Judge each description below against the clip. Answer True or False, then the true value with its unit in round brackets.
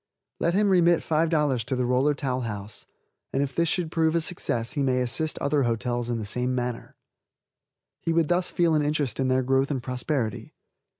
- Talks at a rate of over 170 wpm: True (195 wpm)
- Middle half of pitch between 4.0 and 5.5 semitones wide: True (4.3 semitones)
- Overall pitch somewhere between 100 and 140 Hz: True (135 Hz)